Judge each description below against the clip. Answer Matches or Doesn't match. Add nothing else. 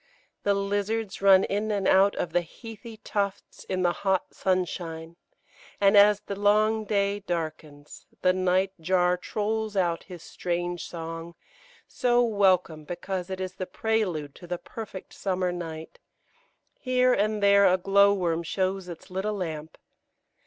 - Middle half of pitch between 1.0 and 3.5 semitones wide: Matches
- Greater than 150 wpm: Doesn't match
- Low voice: Doesn't match